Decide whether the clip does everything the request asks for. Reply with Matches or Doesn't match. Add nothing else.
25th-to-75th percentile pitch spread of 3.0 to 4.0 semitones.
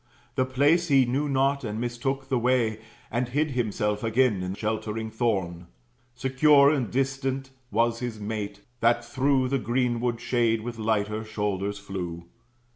Matches